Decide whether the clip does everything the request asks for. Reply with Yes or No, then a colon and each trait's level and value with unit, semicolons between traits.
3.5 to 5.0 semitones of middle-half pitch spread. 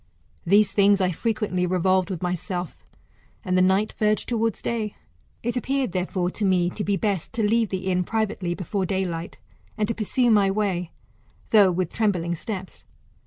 No: average, 2.9 semitones